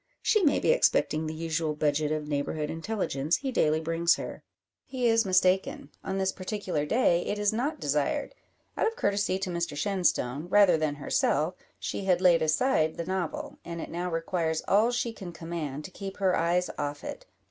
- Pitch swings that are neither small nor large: Yes, average, 4.4 semitones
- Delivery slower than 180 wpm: No, average, 185 wpm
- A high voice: No, medium, 175 Hz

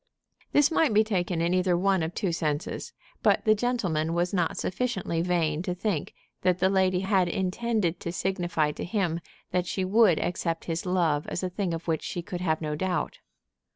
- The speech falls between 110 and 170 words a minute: No, average, 190 wpm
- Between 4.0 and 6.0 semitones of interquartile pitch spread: No, narrow, 2.5 semitones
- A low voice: No, medium, 180 Hz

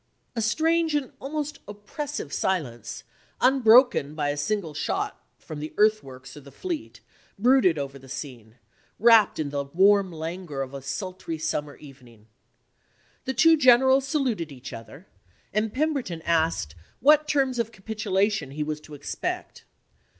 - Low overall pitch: No, high, 190 Hz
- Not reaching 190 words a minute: Yes, average, 145 wpm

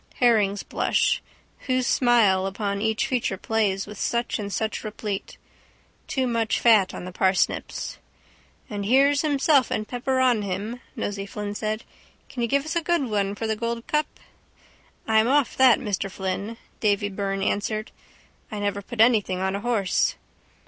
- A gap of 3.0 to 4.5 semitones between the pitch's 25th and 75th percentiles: Yes, average, 3.4 semitones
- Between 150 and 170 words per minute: Yes, average, 160 wpm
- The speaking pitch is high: Yes, high, 215 Hz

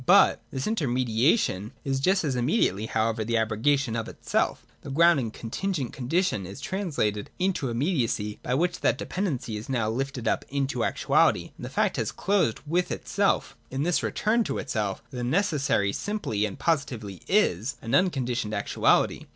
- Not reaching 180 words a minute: Yes, average, 165 wpm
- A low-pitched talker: Yes, low, 130 Hz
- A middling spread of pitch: No, wide, 7.1 semitones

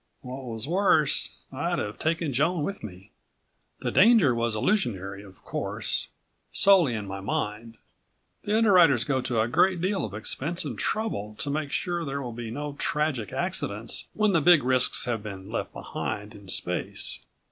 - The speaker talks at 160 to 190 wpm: Yes, average, 170 wpm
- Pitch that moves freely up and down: Yes, wide, 7.6 semitones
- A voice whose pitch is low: Yes, low, 130 Hz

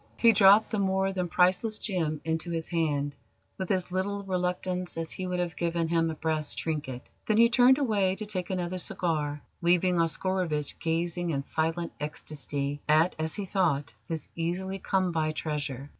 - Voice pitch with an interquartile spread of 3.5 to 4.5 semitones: No, average, 3.1 semitones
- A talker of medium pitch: Yes, medium, 175 Hz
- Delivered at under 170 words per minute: No, average, 175 wpm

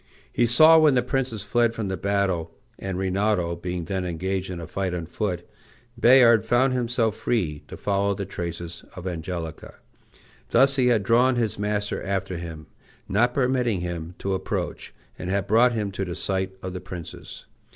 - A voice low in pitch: Yes, low, 100 Hz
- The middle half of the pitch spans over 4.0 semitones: Yes, average, 4.7 semitones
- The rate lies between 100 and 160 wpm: No, average, 175 wpm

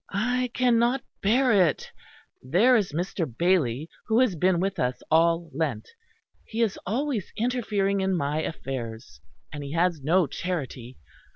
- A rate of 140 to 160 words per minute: Yes, average, 145 wpm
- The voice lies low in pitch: No, medium, 180 Hz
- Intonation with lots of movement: Yes, wide, 6.8 semitones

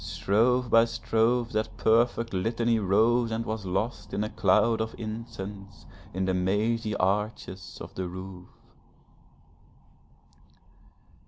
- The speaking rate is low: Yes, slow, 115 wpm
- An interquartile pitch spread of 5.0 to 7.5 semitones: No, average, 3.0 semitones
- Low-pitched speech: Yes, low, 110 Hz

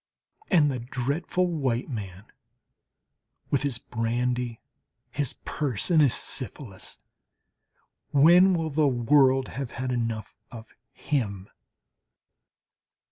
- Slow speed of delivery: Yes, slow, 100 wpm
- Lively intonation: No, average, 4.0 semitones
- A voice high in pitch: No, low, 130 Hz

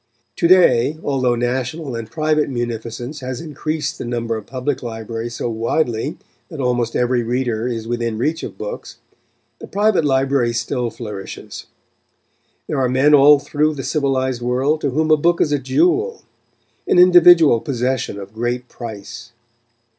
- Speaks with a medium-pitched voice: No, low, 130 Hz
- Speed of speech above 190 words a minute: No, average, 155 wpm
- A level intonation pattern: No, average, 4.2 semitones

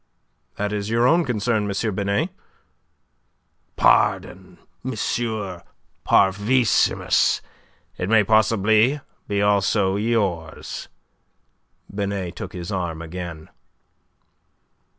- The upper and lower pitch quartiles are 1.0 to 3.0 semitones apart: Yes, average, 2.7 semitones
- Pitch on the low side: Yes, low, 100 Hz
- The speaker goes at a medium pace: No, slow, 85 wpm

